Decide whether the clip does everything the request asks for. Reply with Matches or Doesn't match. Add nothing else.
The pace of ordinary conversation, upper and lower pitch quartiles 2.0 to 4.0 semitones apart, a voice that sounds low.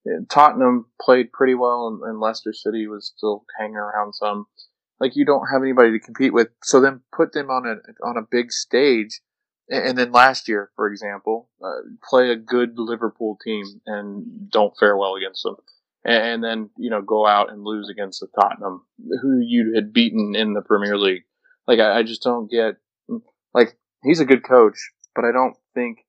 Matches